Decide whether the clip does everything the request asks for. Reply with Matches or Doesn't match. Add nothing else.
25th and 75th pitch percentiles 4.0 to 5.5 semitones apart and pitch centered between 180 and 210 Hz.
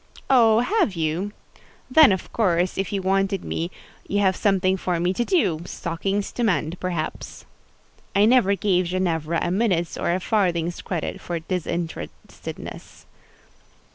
Doesn't match